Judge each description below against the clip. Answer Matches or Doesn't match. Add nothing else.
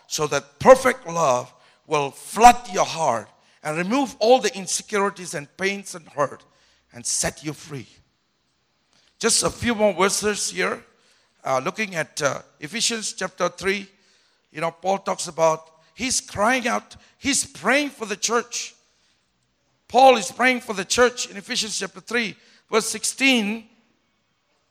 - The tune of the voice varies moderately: Doesn't match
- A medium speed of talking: Matches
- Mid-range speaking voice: Doesn't match